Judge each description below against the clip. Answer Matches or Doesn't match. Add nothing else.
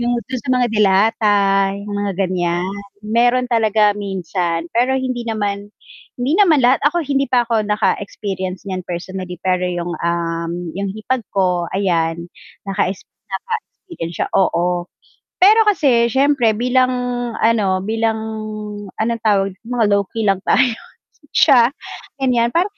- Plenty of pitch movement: Doesn't match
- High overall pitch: Matches